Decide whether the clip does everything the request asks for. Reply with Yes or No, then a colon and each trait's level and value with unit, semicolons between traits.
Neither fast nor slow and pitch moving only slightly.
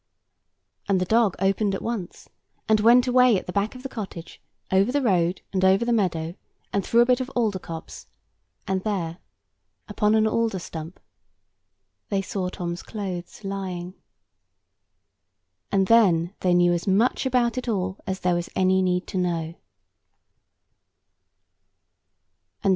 No: average, 150 wpm; average, 3.7 semitones